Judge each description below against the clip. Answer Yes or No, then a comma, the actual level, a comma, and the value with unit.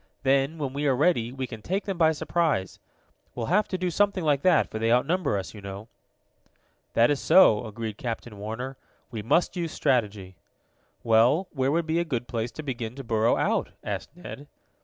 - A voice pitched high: No, low, 130 Hz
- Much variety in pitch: Yes, wide, 6.1 semitones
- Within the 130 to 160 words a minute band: No, average, 195 wpm